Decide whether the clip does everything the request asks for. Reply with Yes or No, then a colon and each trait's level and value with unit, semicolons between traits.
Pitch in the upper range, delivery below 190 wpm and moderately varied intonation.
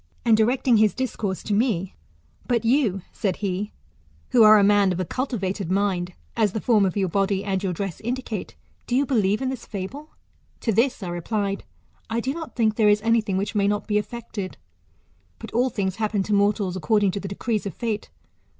No: high, 210 Hz; average, 200 wpm; average, 3.0 semitones